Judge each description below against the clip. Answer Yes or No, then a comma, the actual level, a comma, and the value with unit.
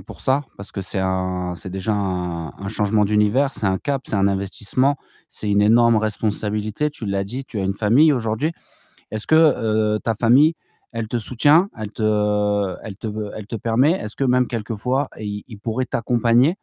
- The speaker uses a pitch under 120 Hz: Yes, low, 110 Hz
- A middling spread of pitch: Yes, average, 3.6 semitones